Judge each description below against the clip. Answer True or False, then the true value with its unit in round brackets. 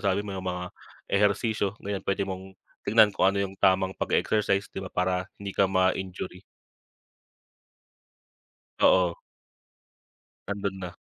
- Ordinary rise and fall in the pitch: False (1.3 semitones)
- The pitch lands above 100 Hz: False (95 Hz)